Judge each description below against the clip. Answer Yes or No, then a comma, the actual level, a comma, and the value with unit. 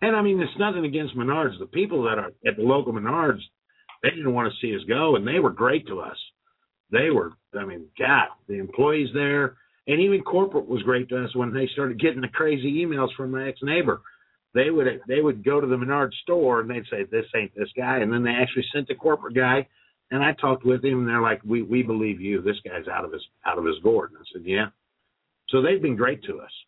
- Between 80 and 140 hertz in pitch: Yes, low, 135 Hz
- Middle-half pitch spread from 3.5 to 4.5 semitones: Yes, average, 4.1 semitones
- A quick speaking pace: Yes, fast, 245 wpm